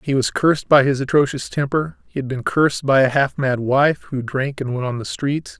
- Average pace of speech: No, fast, 245 wpm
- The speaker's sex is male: Yes, male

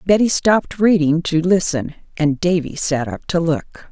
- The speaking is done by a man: No, female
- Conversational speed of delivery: Yes, average, 170 wpm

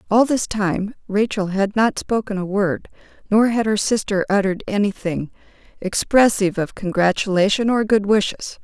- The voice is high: Yes, high, 205 Hz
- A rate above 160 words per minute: No, average, 145 wpm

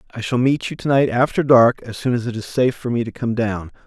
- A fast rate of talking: Yes, fast, 280 wpm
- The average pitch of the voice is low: Yes, low, 120 Hz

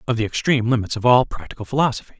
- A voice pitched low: Yes, low, 115 Hz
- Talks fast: Yes, fast, 220 wpm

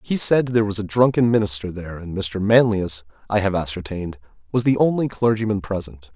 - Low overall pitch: Yes, low, 105 Hz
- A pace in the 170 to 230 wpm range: Yes, average, 185 wpm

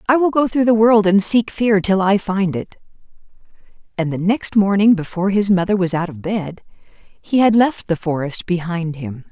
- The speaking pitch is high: Yes, high, 195 Hz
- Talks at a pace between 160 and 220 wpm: Yes, average, 200 wpm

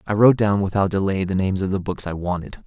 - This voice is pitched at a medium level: No, very low, 95 Hz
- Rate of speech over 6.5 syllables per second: Yes, 6.8 syllables/s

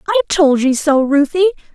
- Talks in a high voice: Yes, very high, 300 Hz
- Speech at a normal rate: Yes, average, 170 wpm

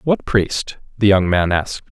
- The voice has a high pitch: No, low, 105 Hz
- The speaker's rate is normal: Yes, average, 180 wpm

